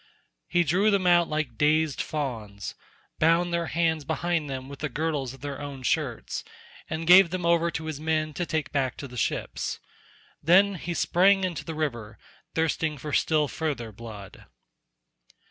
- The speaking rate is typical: Yes, average, 165 wpm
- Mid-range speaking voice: Yes, medium, 155 Hz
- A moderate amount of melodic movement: Yes, average, 3.6 semitones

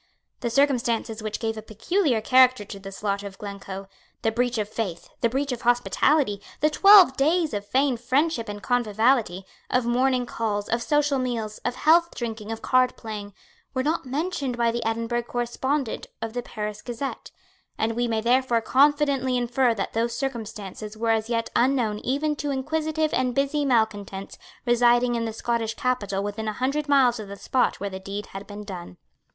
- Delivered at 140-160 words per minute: No, average, 175 wpm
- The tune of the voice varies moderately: Yes, average, 3.5 semitones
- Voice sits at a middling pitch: No, high, 235 Hz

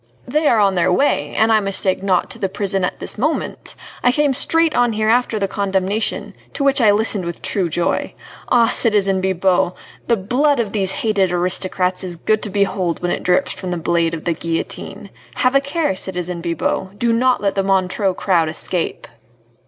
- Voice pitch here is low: No, high, 195 Hz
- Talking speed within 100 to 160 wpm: No, average, 195 wpm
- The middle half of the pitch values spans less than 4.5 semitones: Yes, average, 4.0 semitones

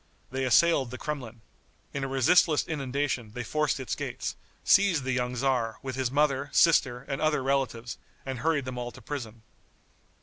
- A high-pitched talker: No, low, 135 Hz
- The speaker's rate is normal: Yes, average, 170 wpm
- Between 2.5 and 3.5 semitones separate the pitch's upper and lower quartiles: Yes, average, 2.9 semitones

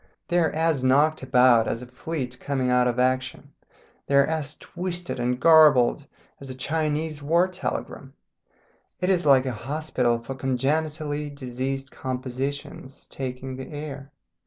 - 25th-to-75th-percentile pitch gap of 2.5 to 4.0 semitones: Yes, average, 3.2 semitones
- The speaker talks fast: No, average, 145 wpm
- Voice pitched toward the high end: No, low, 135 Hz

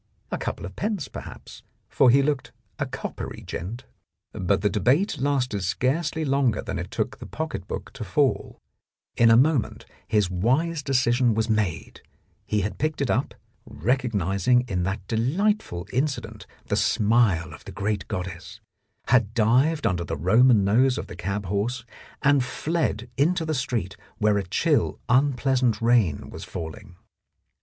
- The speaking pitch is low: Yes, low, 120 Hz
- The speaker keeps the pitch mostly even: No, average, 5.3 semitones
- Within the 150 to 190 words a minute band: Yes, average, 155 wpm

